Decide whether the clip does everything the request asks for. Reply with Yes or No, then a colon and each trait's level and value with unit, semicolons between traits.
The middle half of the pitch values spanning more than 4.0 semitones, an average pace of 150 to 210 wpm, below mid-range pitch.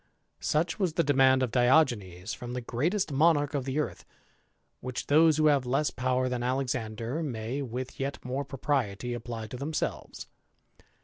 No: average, 3.1 semitones; average, 160 wpm; low, 130 Hz